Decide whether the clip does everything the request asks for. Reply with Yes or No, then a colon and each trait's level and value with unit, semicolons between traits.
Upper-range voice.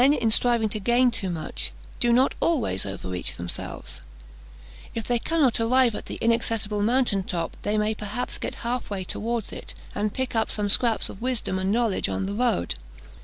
Yes: high, 225 Hz